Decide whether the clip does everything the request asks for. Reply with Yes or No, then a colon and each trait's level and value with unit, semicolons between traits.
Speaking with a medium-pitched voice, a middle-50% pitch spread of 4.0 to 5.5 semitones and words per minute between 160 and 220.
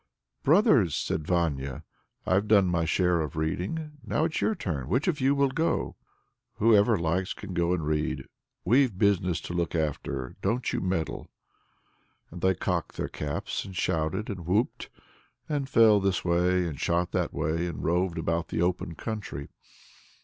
No: very low, 90 Hz; average, 4.7 semitones; average, 165 wpm